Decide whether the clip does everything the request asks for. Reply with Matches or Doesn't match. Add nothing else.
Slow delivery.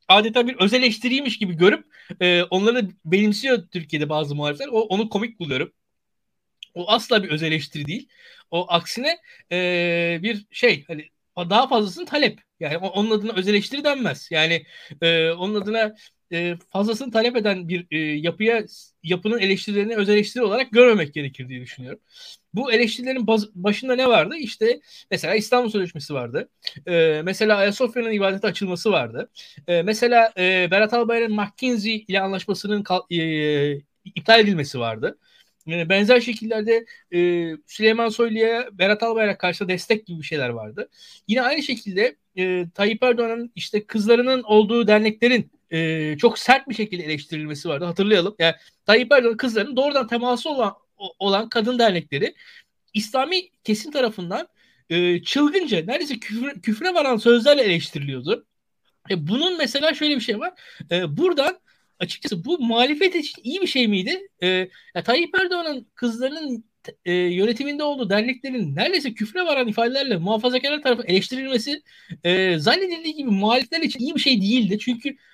Doesn't match